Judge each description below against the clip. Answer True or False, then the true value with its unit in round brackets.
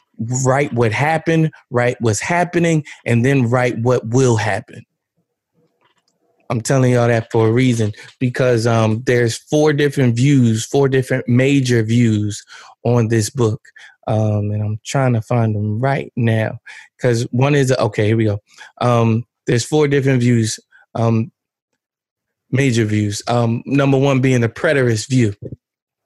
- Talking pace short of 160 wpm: True (145 wpm)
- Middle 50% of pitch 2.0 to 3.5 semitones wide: True (2.8 semitones)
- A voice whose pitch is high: False (120 Hz)